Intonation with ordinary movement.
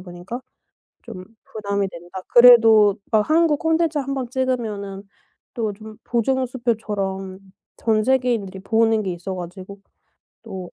Yes: average, 4.3 semitones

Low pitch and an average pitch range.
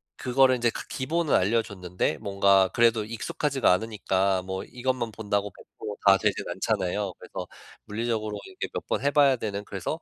Yes: low, 110 Hz; average, 3.8 semitones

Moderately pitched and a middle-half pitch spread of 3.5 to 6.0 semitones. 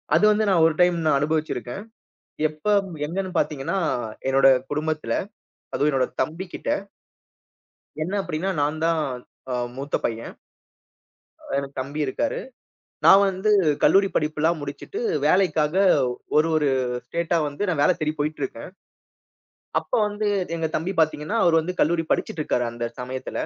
Yes: medium, 155 Hz; average, 4.0 semitones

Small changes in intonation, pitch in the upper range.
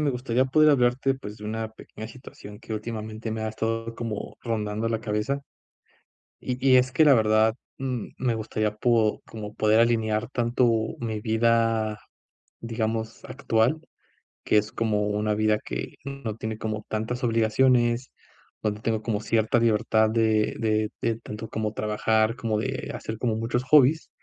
No: narrow, 1.9 semitones; low, 110 Hz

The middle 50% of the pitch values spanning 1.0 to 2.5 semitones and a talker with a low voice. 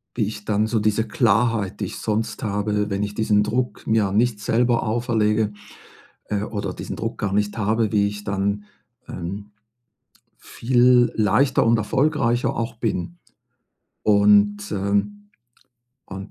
Yes: narrow, 2.0 semitones; low, 105 Hz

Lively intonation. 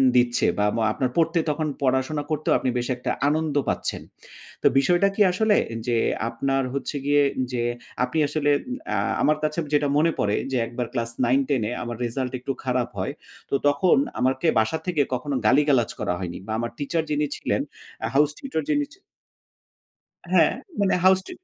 No: average, 3.8 semitones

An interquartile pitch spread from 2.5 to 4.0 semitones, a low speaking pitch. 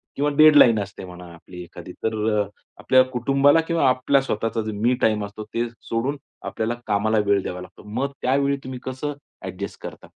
No: average, 4.9 semitones; low, 115 Hz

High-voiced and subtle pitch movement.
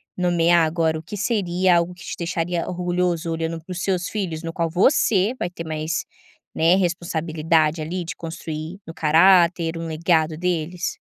No: medium, 170 Hz; narrow, 1.8 semitones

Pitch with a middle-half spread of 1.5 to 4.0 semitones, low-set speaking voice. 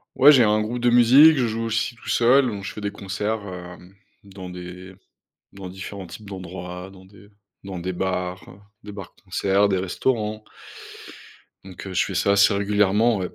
Yes: average, 2.8 semitones; low, 100 Hz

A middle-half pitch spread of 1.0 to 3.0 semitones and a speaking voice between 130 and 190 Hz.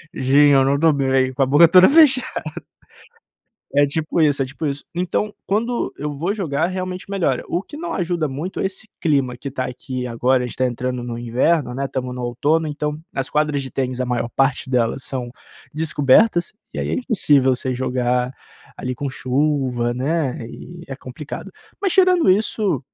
No: average, 4.9 semitones; medium, 140 Hz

